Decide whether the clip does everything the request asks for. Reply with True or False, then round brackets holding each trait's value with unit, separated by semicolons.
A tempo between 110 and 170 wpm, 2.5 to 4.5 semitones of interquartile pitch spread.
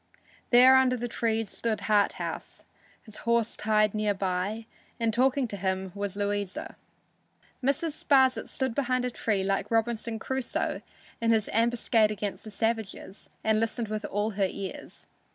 True (150 wpm; 2.8 semitones)